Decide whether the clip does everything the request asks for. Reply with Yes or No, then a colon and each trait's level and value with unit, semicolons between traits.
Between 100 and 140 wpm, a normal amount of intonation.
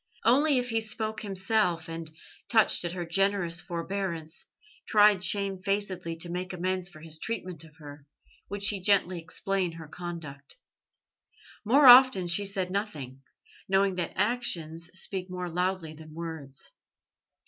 Yes: slow, 135 wpm; average, 3.3 semitones